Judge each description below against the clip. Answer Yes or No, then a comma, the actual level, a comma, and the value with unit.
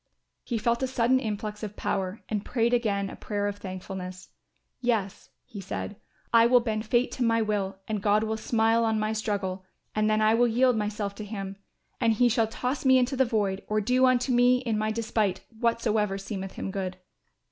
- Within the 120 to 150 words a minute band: No, average, 200 wpm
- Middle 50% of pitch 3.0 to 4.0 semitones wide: No, narrow, 2.6 semitones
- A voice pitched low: No, high, 215 Hz